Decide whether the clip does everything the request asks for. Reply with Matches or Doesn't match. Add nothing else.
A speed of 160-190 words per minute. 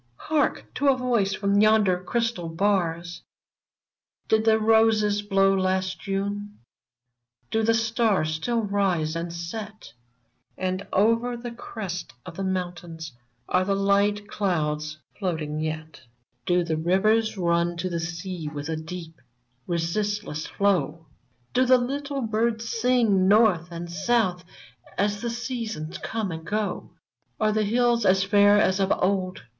Doesn't match